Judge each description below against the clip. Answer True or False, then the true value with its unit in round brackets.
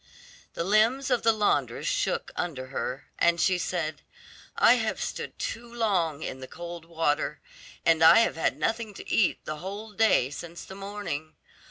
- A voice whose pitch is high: False (175 Hz)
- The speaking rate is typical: True (170 wpm)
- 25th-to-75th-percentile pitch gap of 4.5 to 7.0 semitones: True (5.3 semitones)